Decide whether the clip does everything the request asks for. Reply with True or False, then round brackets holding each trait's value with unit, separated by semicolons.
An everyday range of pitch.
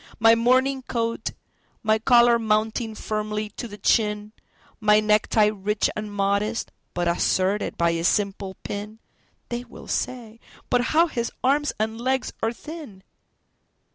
False (2.3 semitones)